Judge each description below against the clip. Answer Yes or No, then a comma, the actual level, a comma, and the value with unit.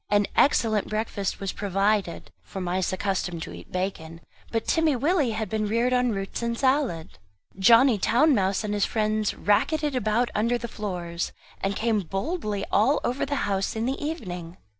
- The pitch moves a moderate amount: Yes, average, 4.0 semitones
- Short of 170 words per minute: No, average, 175 wpm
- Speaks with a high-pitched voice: Yes, high, 215 Hz